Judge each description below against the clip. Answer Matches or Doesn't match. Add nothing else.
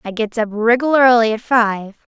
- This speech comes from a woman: Matches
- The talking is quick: Doesn't match